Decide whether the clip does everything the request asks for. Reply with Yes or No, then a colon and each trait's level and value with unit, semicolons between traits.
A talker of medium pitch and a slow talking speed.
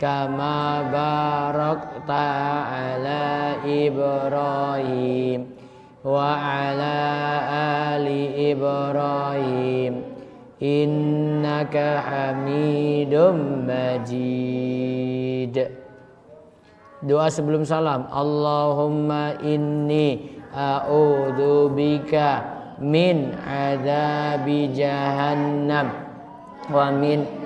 Yes: medium, 145 Hz; slow, 50 wpm